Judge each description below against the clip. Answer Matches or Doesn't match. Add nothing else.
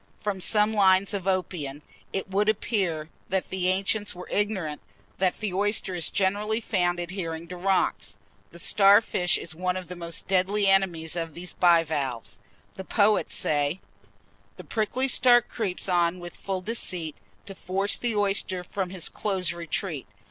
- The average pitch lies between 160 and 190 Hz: Matches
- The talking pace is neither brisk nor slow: Matches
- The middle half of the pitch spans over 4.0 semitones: Doesn't match